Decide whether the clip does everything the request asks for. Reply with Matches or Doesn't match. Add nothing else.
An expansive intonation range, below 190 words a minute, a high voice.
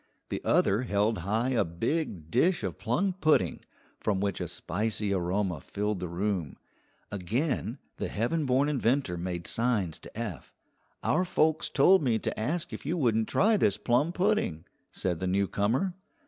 Doesn't match